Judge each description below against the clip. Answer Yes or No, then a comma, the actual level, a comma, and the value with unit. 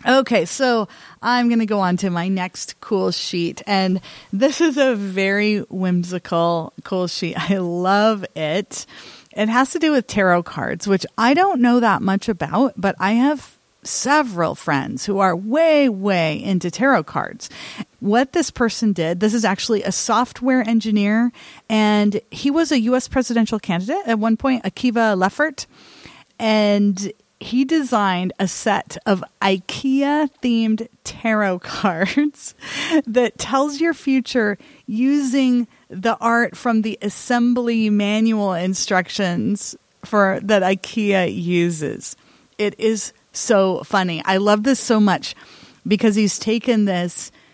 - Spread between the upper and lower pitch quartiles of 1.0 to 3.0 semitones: No, average, 4.4 semitones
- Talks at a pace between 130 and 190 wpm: Yes, average, 140 wpm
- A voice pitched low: No, high, 215 Hz